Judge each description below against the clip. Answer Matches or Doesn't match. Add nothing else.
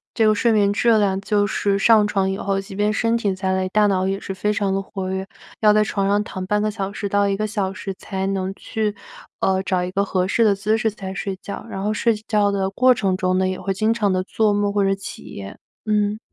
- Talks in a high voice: Matches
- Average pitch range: Doesn't match